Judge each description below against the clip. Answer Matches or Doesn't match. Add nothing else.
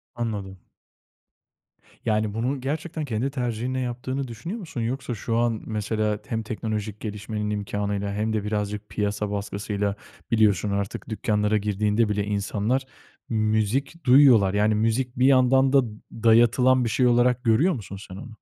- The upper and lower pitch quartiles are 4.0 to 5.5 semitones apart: Doesn't match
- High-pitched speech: Doesn't match